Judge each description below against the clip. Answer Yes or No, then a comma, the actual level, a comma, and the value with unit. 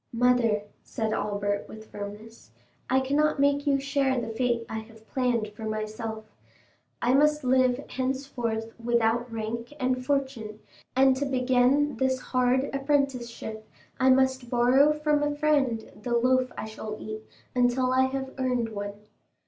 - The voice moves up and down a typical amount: Yes, average, 3.1 semitones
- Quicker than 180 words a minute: No, average, 145 wpm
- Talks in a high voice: Yes, very high, 250 Hz